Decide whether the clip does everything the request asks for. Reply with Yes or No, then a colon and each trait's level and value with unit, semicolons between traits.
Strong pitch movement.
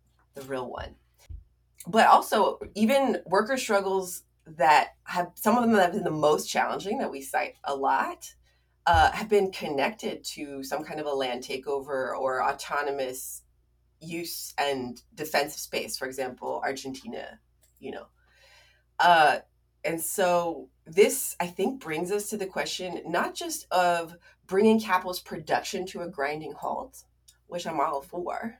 Yes: wide, 6.4 semitones